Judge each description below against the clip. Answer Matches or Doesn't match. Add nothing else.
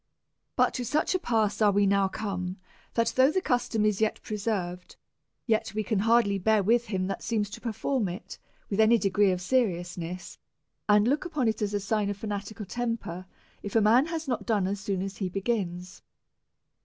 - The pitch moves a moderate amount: Matches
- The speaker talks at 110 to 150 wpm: Doesn't match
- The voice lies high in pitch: Matches